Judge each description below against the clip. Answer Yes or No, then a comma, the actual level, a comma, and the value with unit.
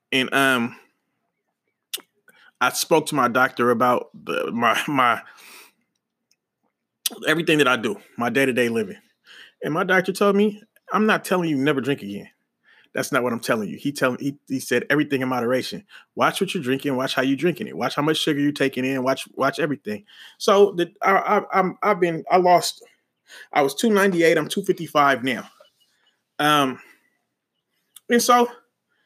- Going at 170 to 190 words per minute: Yes, average, 180 wpm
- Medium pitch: Yes, medium, 150 Hz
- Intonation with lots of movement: Yes, wide, 6.1 semitones